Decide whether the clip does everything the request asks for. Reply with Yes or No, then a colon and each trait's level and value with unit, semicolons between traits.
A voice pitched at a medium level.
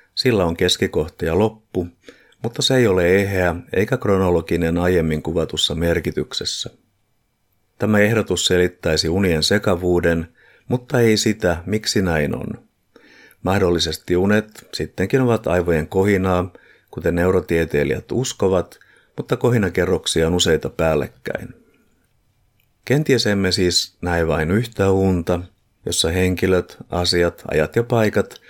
No: very low, 95 Hz